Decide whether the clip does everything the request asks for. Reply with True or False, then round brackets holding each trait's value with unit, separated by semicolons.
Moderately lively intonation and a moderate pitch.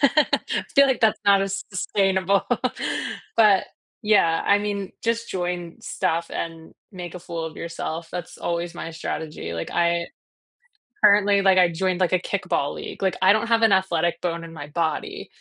True (3.1 semitones; 180 Hz)